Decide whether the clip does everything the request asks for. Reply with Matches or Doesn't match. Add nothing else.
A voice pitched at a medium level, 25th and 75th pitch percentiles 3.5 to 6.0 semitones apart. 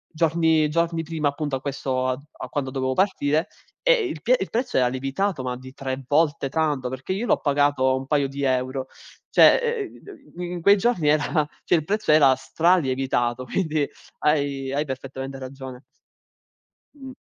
Matches